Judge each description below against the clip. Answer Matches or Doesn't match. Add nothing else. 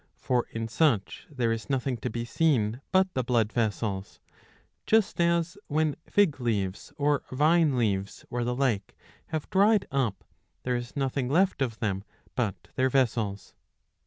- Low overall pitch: Matches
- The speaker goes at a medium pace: Matches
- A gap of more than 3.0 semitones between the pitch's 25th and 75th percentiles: Matches